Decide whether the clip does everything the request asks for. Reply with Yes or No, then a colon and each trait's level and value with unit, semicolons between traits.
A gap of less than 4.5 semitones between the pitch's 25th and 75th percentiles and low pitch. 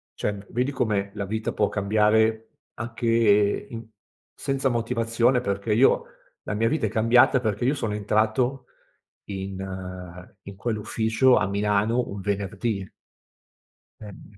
Yes: narrow, 2.6 semitones; low, 110 Hz